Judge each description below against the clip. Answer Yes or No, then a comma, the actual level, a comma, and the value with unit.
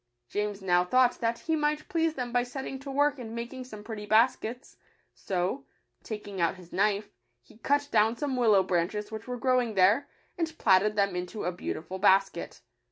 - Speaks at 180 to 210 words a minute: Yes, average, 185 wpm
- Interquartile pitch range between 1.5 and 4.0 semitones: No, average, 4.6 semitones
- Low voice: No, high, 220 Hz